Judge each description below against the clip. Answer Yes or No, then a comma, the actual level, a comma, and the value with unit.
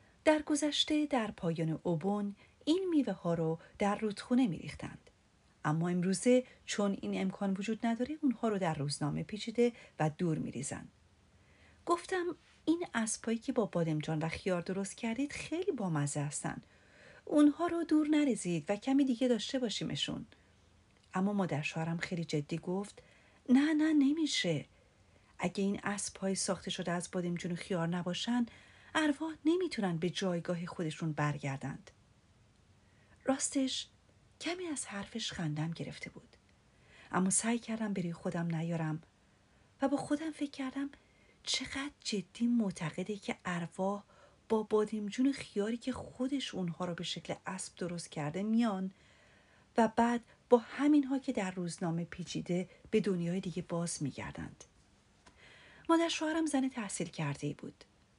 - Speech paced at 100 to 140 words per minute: Yes, average, 135 wpm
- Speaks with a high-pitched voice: Yes, high, 195 Hz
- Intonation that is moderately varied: No, wide, 7.1 semitones